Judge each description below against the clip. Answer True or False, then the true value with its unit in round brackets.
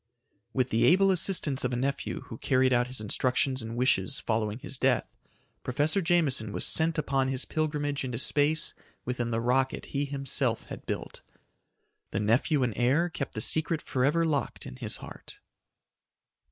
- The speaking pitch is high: False (130 Hz)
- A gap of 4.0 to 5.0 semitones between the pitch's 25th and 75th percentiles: False (3.4 semitones)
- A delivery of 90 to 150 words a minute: False (165 wpm)